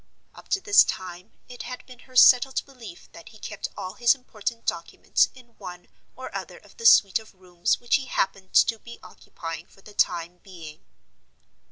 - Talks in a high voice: Yes, high, 215 Hz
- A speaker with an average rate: Yes, average, 185 wpm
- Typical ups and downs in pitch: No, wide, 5.8 semitones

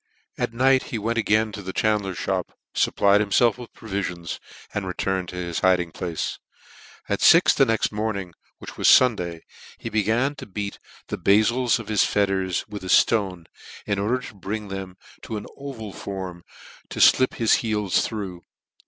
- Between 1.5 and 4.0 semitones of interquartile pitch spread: Yes, average, 3.0 semitones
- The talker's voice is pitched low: Yes, low, 100 Hz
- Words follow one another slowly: No, average, 170 wpm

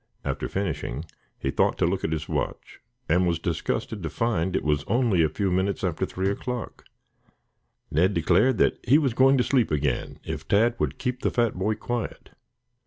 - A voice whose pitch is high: No, very low, 95 Hz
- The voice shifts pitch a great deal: Yes, wide, 6.2 semitones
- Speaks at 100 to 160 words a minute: No, average, 185 wpm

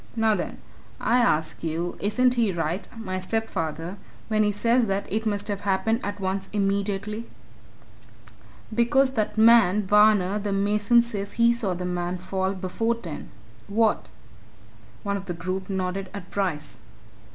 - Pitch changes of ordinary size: Yes, average, 3.1 semitones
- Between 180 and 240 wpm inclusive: No, average, 150 wpm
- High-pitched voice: Yes, high, 200 Hz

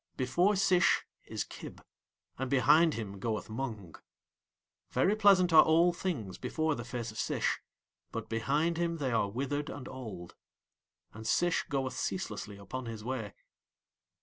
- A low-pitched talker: Yes, low, 130 Hz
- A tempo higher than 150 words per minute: No, average, 145 wpm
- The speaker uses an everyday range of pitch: No, wide, 6.8 semitones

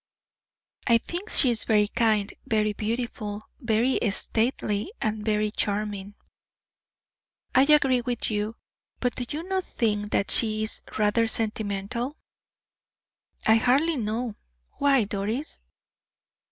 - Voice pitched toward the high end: Yes, high, 220 Hz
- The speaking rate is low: Yes, slow, 115 wpm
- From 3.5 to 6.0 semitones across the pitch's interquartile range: No, average, 3.0 semitones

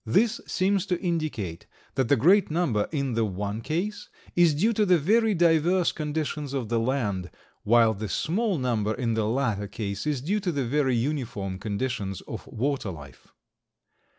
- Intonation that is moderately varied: No, wide, 7.8 semitones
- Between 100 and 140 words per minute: No, average, 170 wpm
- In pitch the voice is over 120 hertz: Yes, low, 135 Hz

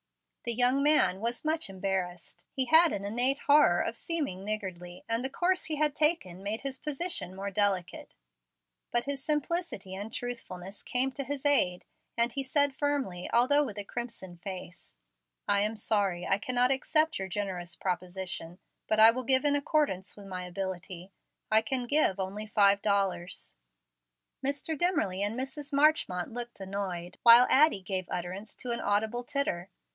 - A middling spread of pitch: No, wide, 6.6 semitones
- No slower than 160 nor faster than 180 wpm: Yes, average, 165 wpm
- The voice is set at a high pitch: Yes, high, 220 Hz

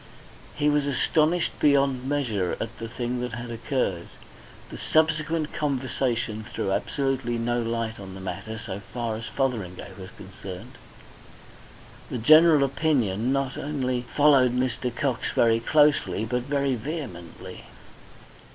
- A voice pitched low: Yes, low, 125 Hz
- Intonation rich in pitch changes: No, average, 4.0 semitones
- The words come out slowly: Yes, slow, 130 wpm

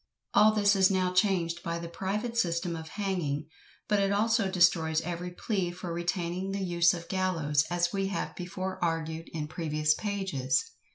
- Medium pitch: Yes, medium, 175 Hz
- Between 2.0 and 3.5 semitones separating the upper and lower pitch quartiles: Yes, narrow, 2.6 semitones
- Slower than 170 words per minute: No, average, 175 wpm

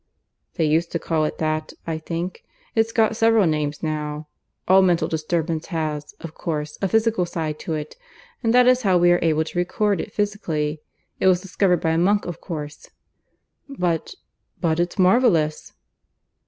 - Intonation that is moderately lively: Yes, average, 3.7 semitones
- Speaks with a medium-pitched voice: Yes, medium, 170 Hz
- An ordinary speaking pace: Yes, average, 170 wpm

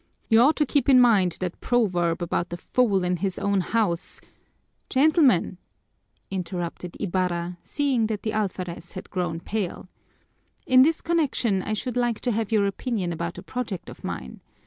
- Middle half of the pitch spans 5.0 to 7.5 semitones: Yes, wide, 5.5 semitones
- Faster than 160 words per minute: Yes, average, 170 wpm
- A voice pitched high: Yes, high, 200 Hz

